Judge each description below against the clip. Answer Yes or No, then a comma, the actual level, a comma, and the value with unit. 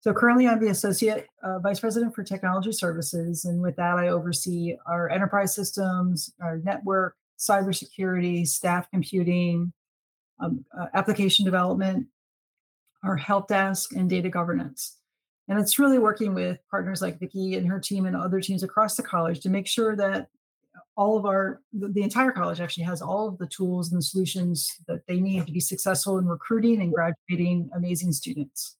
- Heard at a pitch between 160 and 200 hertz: Yes, high, 190 Hz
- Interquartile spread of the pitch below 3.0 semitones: Yes, narrow, 2.4 semitones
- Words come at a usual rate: Yes, average, 175 wpm